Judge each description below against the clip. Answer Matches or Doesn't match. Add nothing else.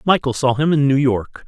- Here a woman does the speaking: Doesn't match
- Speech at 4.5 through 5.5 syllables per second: Matches